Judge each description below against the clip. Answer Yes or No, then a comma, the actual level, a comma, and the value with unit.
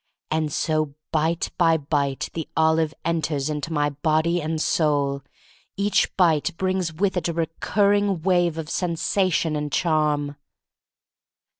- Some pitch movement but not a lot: No, narrow, 2.3 semitones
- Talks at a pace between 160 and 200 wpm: No, slow, 135 wpm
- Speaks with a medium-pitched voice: Yes, medium, 160 Hz